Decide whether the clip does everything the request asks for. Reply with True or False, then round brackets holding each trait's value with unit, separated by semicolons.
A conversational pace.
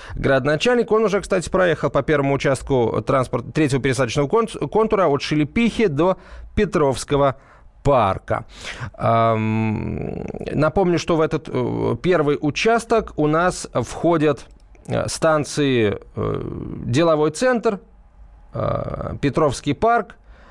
False (90 wpm)